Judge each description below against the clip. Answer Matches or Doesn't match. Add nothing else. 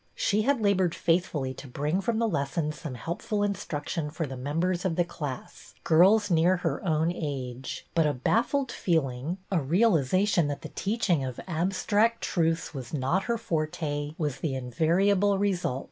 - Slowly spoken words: Doesn't match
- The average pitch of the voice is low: Doesn't match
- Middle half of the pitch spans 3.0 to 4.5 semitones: Doesn't match